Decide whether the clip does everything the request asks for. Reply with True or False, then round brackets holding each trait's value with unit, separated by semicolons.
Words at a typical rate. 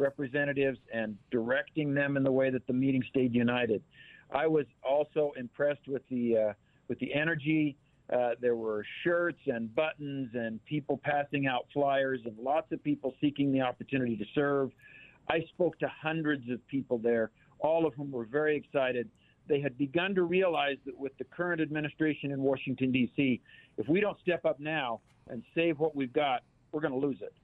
True (185 wpm)